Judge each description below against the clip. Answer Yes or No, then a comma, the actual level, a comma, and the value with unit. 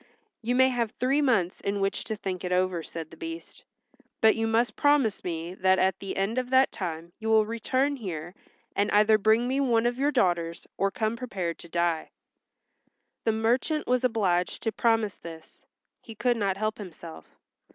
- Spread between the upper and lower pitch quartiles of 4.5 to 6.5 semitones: Yes, average, 4.9 semitones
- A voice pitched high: Yes, high, 215 Hz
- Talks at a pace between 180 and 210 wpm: Yes, average, 185 wpm